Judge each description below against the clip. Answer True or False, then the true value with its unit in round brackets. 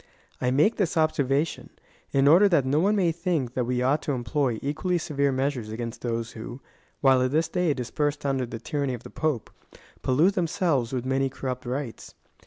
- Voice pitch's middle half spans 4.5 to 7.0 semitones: False (3.8 semitones)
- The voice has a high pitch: False (140 Hz)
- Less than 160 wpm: False (190 wpm)